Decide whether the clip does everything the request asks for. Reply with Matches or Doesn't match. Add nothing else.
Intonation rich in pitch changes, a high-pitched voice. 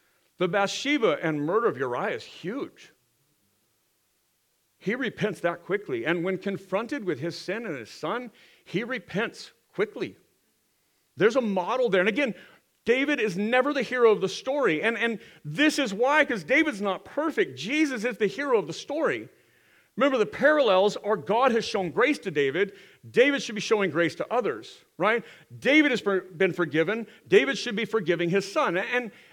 Matches